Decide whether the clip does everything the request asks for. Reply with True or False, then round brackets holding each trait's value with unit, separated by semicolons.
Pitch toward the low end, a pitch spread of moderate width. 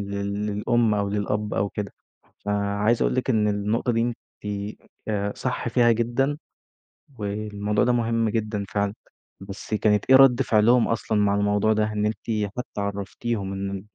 False (105 Hz; 2.3 semitones)